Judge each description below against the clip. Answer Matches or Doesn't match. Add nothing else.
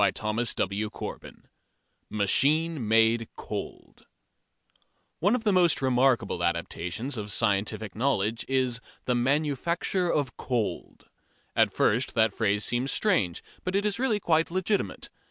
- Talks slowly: Matches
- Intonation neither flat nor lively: Doesn't match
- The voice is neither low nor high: Doesn't match